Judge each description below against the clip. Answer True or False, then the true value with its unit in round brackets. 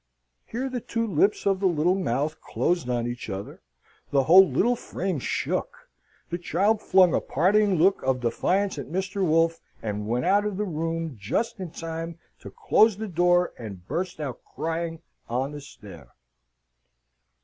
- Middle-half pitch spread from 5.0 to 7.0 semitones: True (5.5 semitones)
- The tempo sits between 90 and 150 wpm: False (165 wpm)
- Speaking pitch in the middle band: True (170 Hz)